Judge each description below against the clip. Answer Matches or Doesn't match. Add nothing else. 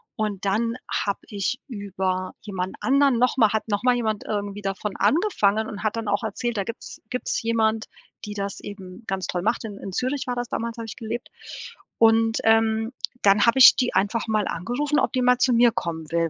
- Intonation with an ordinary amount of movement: Matches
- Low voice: Doesn't match